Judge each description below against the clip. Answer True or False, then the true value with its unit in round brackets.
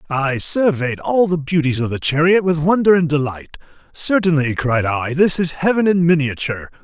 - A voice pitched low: False (155 Hz)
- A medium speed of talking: True (175 wpm)